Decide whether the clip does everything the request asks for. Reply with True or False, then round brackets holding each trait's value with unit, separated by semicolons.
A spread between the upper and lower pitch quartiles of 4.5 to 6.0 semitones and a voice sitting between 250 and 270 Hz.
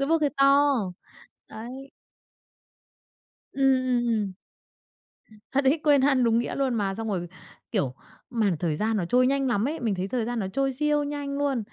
False (4.1 semitones; 255 Hz)